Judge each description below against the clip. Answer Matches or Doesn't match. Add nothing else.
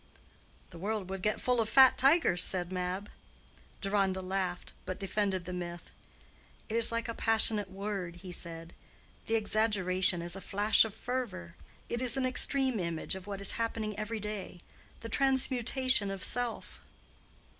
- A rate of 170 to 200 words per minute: Doesn't match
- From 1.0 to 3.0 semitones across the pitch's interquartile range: Doesn't match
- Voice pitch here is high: Matches